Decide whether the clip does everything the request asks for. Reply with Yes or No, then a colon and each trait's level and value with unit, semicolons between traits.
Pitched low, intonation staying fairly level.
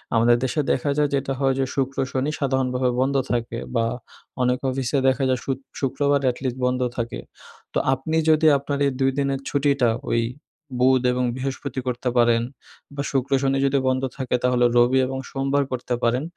Yes: low, 130 Hz; narrow, 1.6 semitones